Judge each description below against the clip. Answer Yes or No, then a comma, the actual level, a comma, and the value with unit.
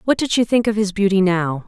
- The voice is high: Yes, high, 200 Hz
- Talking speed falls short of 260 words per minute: No, fast, 285 wpm